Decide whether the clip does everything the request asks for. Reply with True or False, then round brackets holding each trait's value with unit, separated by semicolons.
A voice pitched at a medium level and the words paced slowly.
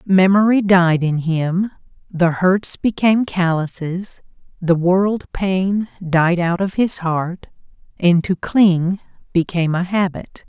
True (180 Hz; 125 wpm)